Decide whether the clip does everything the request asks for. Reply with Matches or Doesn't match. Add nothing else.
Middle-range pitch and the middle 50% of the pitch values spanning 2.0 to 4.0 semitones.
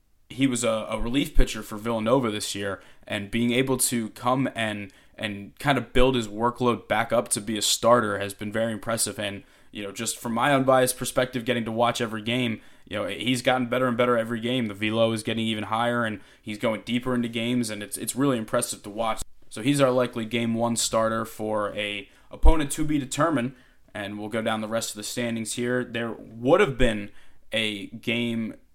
Doesn't match